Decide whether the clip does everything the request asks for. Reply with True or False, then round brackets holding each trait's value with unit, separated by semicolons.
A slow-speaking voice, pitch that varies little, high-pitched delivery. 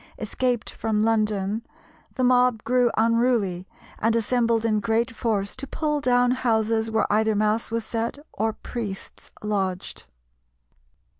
True (130 wpm; 2.2 semitones; 225 Hz)